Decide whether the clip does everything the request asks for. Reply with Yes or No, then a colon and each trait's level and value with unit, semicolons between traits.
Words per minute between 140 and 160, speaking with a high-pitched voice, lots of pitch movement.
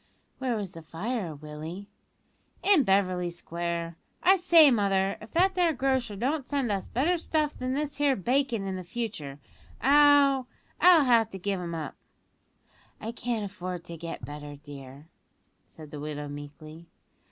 Yes: average, 150 wpm; high, 200 Hz; wide, 8.3 semitones